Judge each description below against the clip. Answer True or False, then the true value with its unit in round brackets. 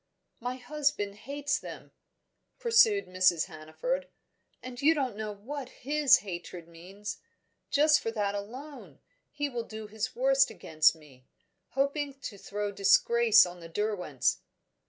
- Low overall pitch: False (220 Hz)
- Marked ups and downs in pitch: True (6.3 semitones)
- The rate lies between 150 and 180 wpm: False (135 wpm)